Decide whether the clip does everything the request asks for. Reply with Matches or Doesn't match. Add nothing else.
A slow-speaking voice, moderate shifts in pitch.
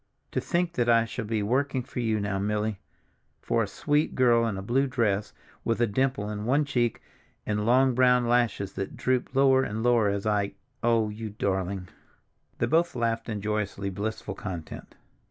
Doesn't match